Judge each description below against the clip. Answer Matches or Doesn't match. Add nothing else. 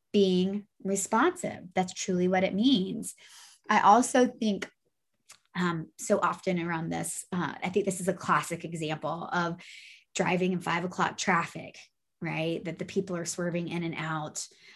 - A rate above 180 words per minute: Doesn't match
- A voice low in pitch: Doesn't match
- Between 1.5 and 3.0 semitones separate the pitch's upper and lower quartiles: Matches